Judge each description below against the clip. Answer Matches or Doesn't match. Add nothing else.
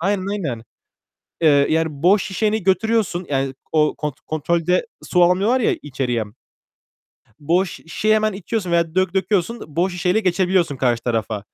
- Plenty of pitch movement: Doesn't match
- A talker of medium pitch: Matches